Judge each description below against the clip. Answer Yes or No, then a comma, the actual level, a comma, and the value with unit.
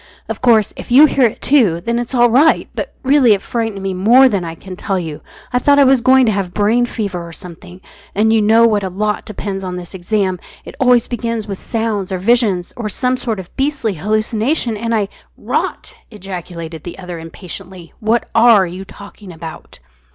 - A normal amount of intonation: Yes, average, 4.4 semitones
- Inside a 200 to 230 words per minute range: Yes, fast, 205 wpm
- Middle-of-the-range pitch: No, high, 210 Hz